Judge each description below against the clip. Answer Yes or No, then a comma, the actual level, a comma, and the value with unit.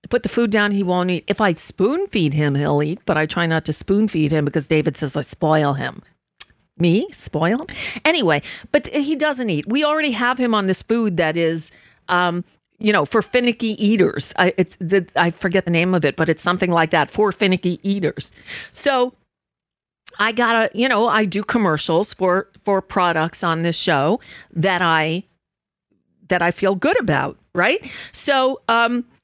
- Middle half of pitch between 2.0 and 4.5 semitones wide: No, wide, 5.4 semitones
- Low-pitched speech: No, high, 190 Hz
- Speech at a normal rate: Yes, average, 190 wpm